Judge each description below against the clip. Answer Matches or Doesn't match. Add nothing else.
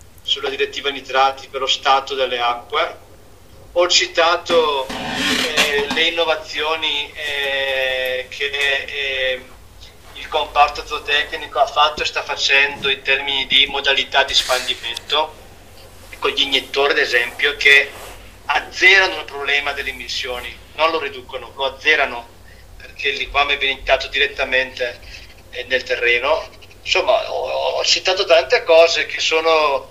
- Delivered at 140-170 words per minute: Doesn't match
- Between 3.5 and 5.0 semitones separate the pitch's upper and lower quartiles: Matches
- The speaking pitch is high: Doesn't match